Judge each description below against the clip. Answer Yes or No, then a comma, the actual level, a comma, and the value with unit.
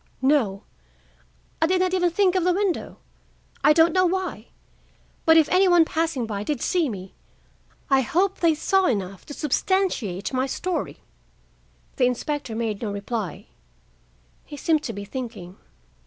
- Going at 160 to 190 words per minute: No, average, 145 wpm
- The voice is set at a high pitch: Yes, very high, 295 Hz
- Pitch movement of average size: No, wide, 8.2 semitones